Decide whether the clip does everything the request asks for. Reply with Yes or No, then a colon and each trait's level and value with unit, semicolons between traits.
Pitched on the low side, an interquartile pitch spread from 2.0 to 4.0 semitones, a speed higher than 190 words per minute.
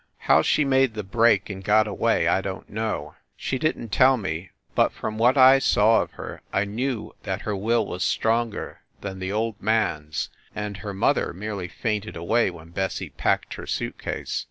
Yes: low, 105 Hz; average, 3.2 semitones; average, 200 wpm